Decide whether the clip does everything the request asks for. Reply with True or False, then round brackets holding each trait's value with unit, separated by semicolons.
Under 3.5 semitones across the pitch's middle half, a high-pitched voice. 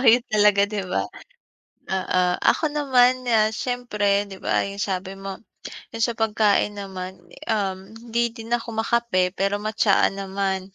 True (2.9 semitones; 205 Hz)